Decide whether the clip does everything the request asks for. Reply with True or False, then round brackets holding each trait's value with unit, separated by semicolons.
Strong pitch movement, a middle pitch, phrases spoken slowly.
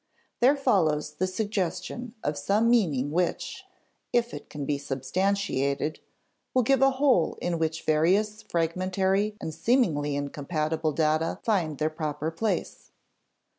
True (5.7 semitones; 170 Hz; 130 wpm)